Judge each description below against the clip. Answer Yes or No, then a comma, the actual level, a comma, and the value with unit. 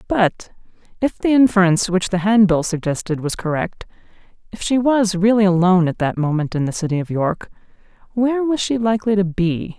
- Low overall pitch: No, high, 195 Hz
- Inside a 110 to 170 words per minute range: Yes, average, 165 wpm